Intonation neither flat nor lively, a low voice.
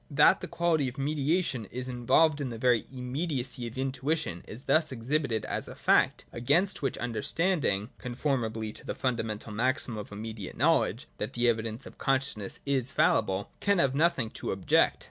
Yes: average, 4.1 semitones; low, 130 Hz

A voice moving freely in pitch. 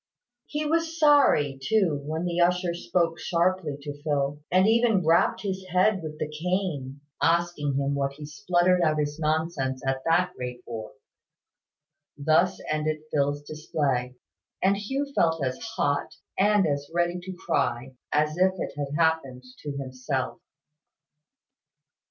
No: average, 4.3 semitones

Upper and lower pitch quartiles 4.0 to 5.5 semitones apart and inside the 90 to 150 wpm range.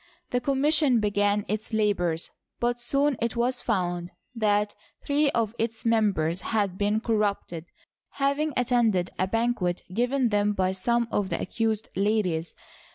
No: average, 3.4 semitones; average, 140 wpm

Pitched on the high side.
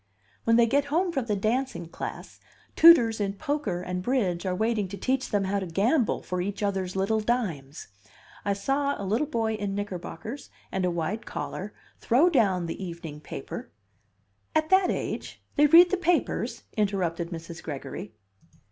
Yes: high, 205 Hz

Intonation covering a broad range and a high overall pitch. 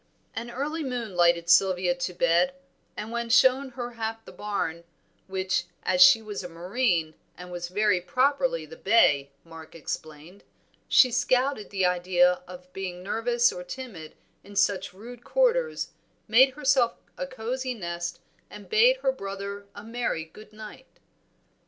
Yes: wide, 5.9 semitones; high, 205 Hz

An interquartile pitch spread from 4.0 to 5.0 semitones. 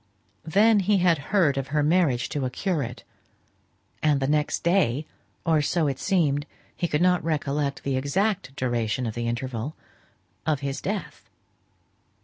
Yes: average, 4.6 semitones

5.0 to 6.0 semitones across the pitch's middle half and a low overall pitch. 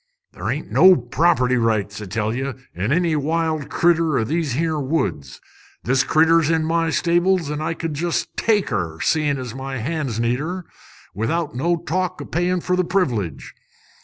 No: wide, 5.4 semitones; medium, 155 Hz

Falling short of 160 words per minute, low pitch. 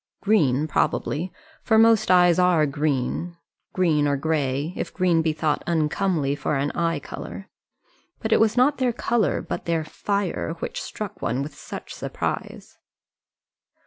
No: average, 145 wpm; medium, 165 Hz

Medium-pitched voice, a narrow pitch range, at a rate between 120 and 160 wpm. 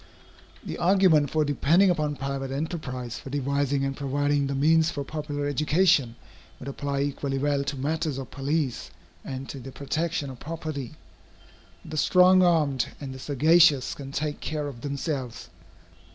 Yes: medium, 145 Hz; narrow, 2.3 semitones; average, 150 wpm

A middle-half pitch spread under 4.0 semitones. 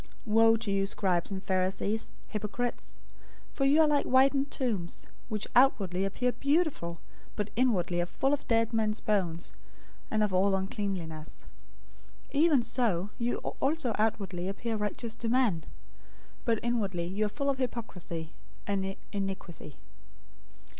No: average, 4.4 semitones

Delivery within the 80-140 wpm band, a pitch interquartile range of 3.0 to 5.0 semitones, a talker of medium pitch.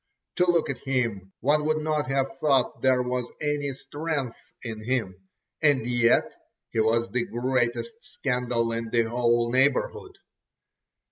No: slow, 135 wpm; average, 3.6 semitones; low, 125 Hz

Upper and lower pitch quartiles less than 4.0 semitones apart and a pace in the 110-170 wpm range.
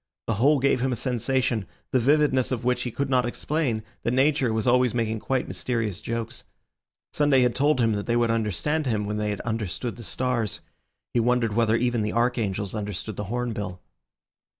No: average, 2.7 semitones; average, 190 wpm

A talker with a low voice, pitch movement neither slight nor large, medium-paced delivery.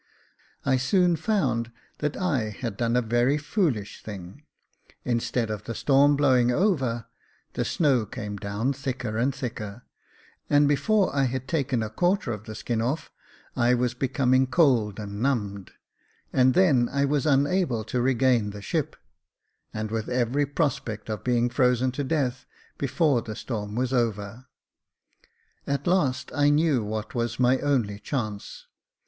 Yes: low, 125 Hz; average, 3.9 semitones; average, 150 wpm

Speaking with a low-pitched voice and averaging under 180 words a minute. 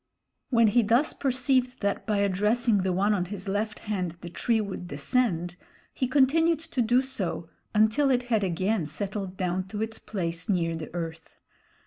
No: high, 205 Hz; average, 170 wpm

